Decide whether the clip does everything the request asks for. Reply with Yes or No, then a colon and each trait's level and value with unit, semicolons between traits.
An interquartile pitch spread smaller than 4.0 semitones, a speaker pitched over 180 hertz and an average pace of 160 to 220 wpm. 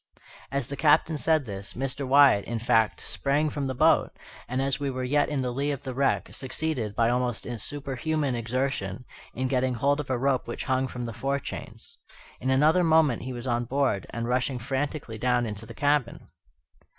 No: average, 2.7 semitones; low, 130 Hz; average, 190 wpm